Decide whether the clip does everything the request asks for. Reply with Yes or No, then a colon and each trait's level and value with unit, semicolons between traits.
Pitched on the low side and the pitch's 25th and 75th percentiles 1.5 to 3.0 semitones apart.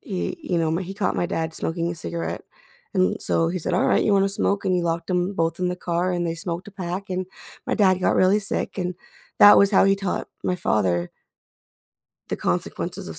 No: medium, 180 Hz; narrow, 2.4 semitones